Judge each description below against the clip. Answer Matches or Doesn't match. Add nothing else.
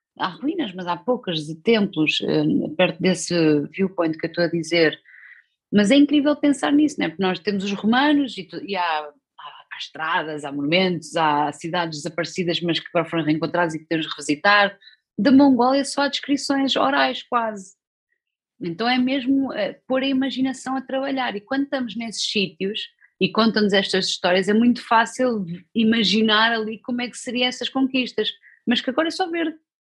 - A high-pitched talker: Matches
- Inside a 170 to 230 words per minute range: Matches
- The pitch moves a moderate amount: Doesn't match